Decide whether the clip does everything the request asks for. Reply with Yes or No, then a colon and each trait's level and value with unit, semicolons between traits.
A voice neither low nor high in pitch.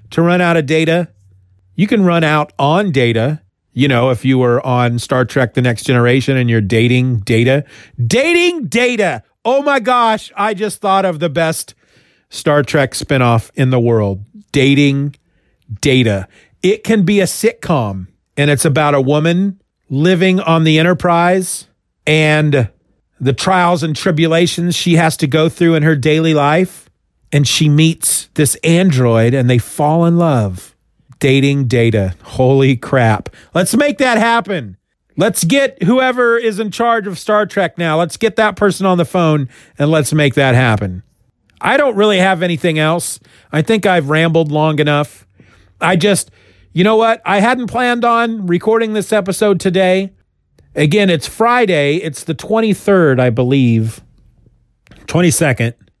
Yes: medium, 155 Hz